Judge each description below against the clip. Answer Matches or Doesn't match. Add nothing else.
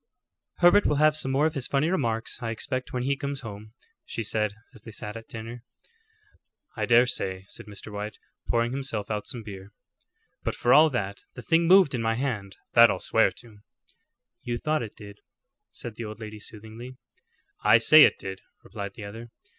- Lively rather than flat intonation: Doesn't match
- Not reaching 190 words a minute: Doesn't match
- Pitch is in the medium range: Doesn't match